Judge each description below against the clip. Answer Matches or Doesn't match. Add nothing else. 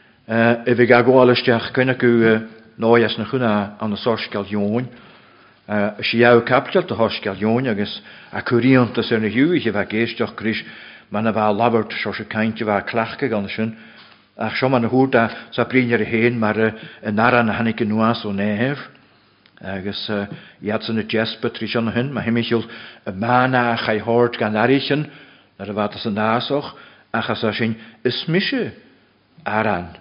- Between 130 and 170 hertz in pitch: Doesn't match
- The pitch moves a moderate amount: Doesn't match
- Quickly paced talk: Doesn't match